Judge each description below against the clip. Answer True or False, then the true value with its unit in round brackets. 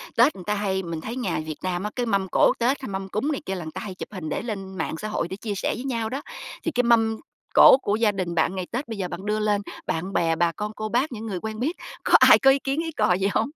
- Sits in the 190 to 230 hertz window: True (210 Hz)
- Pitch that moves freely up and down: False (4.0 semitones)